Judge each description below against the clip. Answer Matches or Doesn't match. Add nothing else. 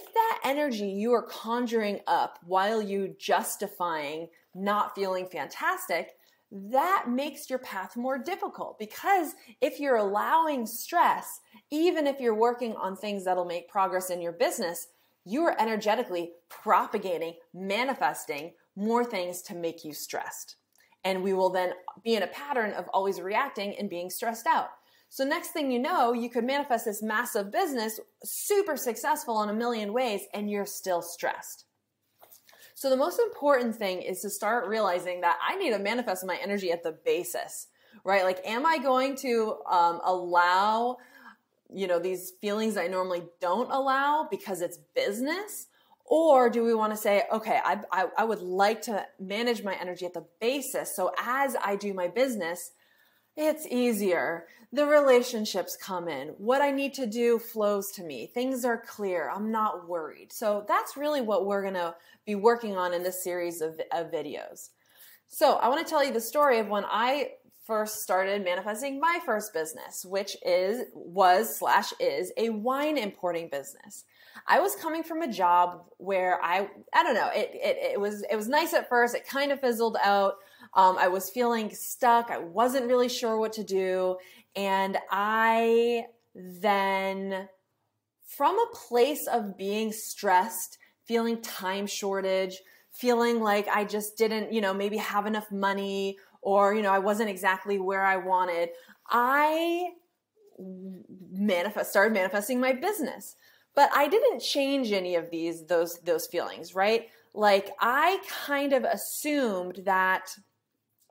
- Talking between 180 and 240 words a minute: Doesn't match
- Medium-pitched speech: Doesn't match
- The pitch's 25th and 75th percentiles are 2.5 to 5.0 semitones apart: Doesn't match